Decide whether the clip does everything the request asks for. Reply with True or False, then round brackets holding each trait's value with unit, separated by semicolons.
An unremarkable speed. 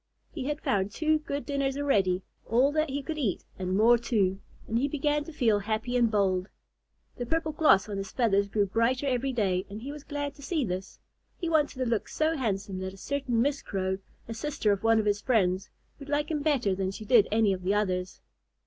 False (220 wpm)